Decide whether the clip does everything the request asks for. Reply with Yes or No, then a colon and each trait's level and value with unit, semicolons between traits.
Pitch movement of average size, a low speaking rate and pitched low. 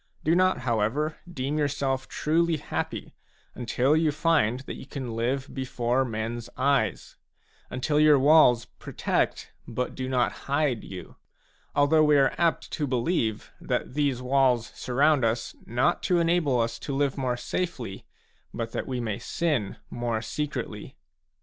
No: average, 3.9 semitones; average, 145 wpm; low, 130 Hz